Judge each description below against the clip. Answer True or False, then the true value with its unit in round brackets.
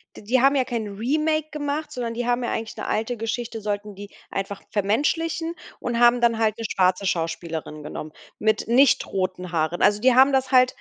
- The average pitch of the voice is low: False (230 Hz)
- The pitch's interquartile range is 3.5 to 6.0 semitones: True (4.3 semitones)